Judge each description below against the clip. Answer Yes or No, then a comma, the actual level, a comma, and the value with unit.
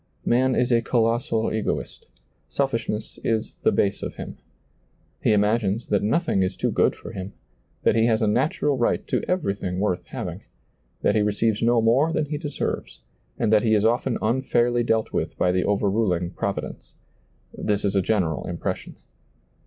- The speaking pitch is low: Yes, low, 110 Hz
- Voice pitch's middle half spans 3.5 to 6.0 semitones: No, average, 2.9 semitones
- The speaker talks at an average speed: Yes, average, 170 wpm